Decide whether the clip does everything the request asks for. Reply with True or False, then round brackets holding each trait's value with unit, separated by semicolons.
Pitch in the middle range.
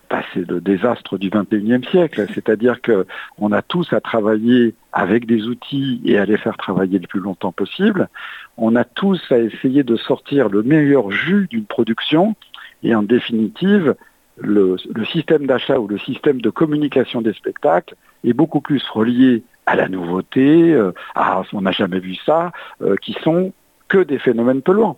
False (120 Hz)